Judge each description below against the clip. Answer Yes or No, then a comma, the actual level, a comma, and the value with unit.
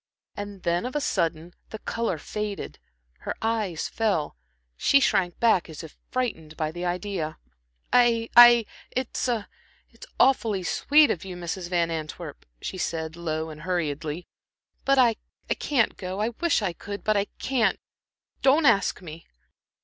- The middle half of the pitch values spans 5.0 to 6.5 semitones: Yes, wide, 5.6 semitones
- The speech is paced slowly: No, average, 155 wpm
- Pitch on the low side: No, high, 190 Hz